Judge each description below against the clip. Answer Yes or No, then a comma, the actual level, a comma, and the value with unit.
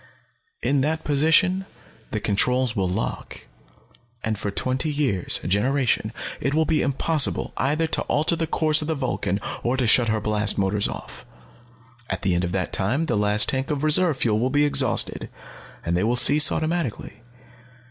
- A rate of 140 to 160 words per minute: No, average, 175 wpm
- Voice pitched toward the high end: No, low, 130 Hz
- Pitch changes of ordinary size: No, wide, 6.3 semitones